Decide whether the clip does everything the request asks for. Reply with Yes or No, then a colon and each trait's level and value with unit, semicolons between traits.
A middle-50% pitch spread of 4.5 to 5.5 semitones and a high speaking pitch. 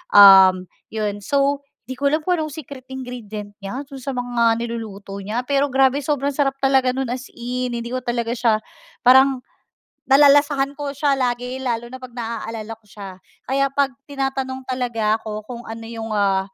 No: average, 3.3 semitones; very high, 250 Hz